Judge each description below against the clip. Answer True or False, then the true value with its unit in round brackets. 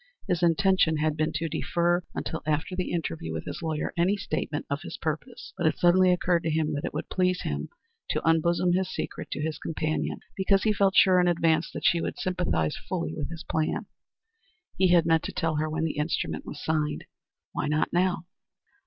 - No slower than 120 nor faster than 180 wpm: False (205 wpm)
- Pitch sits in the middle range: True (165 Hz)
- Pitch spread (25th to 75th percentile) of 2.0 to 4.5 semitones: True (2.4 semitones)